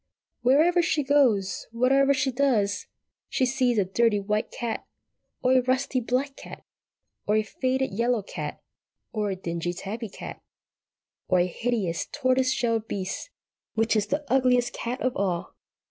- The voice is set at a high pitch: Yes, high, 240 Hz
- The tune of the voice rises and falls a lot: No, average, 4.1 semitones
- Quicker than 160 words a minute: No, average, 150 wpm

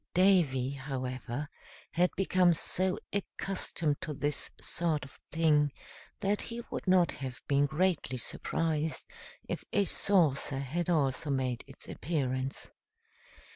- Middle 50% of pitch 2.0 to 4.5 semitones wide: No, average, 4.9 semitones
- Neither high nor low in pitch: Yes, medium, 150 Hz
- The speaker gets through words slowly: Yes, slow, 120 wpm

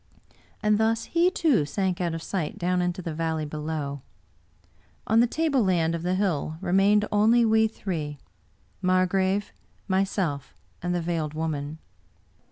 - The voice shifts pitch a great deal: No, average, 4.4 semitones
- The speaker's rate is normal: Yes, average, 150 wpm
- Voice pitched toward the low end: No, medium, 185 Hz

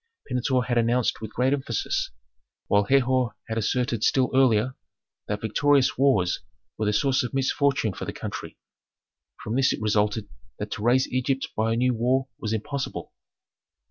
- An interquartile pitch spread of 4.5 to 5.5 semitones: No, average, 3.2 semitones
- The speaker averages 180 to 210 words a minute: No, average, 160 wpm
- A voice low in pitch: Yes, low, 125 Hz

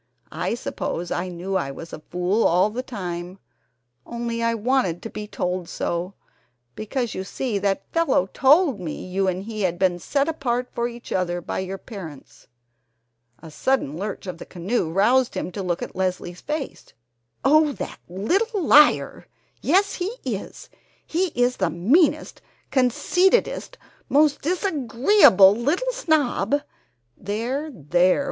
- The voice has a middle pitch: No, high, 215 Hz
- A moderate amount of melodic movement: No, wide, 7.5 semitones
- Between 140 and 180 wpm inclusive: Yes, average, 150 wpm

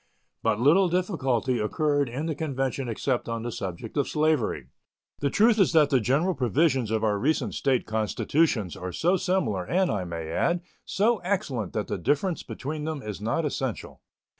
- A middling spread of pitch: No, wide, 6.6 semitones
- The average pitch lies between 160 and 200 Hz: No, low, 135 Hz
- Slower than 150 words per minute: No, average, 175 wpm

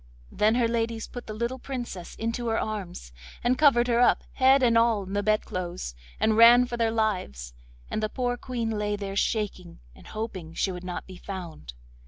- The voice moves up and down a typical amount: Yes, average, 4.0 semitones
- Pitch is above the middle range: Yes, high, 220 Hz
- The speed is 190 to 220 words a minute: Yes, average, 195 wpm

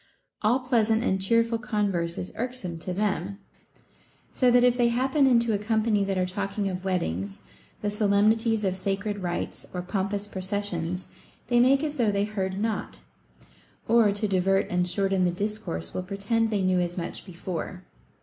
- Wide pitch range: No, average, 3.4 semitones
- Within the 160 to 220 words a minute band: Yes, average, 170 wpm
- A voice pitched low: No, high, 200 Hz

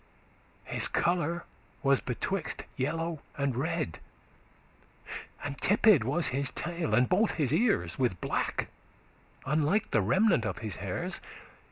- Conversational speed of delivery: No, slow, 125 wpm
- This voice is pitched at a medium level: Yes, medium, 150 Hz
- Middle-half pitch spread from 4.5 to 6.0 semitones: Yes, average, 5.0 semitones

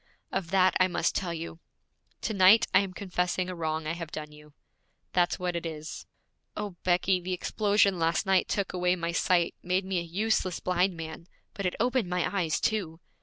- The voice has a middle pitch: Yes, medium, 180 Hz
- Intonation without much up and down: Yes, narrow, 2.3 semitones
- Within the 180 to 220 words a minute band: Yes, average, 195 wpm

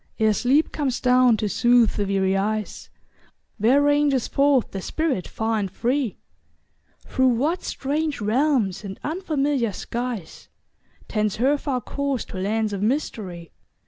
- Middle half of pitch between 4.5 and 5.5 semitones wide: Yes, average, 5.1 semitones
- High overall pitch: Yes, high, 240 Hz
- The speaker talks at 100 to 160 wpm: Yes, average, 140 wpm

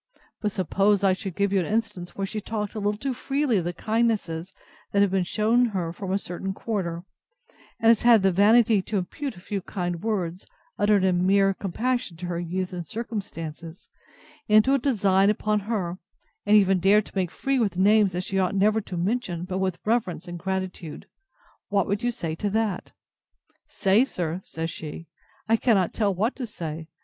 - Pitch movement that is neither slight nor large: Yes, average, 3.3 semitones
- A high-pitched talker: Yes, high, 195 Hz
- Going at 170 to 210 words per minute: Yes, average, 195 wpm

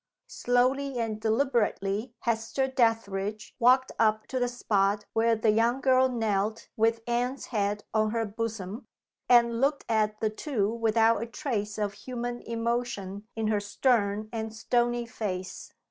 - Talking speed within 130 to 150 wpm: Yes, average, 145 wpm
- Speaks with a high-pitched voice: Yes, high, 225 Hz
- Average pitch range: No, narrow, 2.3 semitones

